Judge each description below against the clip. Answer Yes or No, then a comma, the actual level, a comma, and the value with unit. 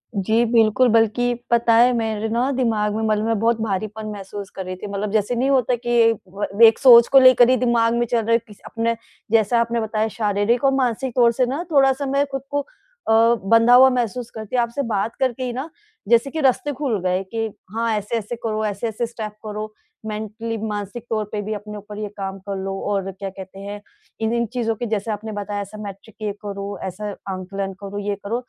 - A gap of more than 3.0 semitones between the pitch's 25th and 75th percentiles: No, average, 2.7 semitones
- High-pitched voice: Yes, high, 225 Hz